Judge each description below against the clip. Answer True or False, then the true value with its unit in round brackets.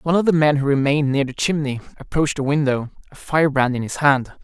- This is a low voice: False (145 Hz)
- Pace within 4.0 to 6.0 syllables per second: False (6.5 syllables/s)